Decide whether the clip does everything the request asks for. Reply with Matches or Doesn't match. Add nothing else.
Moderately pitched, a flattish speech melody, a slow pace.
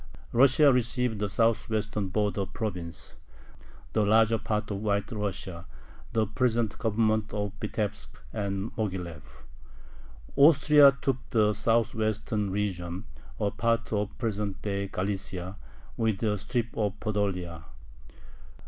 Doesn't match